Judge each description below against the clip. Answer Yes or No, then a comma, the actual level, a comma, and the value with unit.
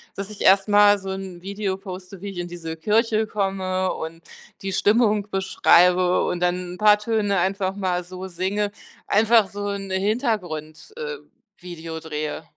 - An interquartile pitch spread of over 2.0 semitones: Yes, narrow, 2.5 semitones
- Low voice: No, high, 190 Hz